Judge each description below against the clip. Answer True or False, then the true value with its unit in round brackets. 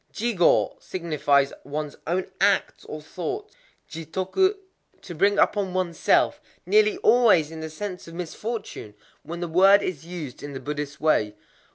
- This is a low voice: False (175 Hz)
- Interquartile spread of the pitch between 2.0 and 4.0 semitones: False (4.8 semitones)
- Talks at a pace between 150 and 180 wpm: False (140 wpm)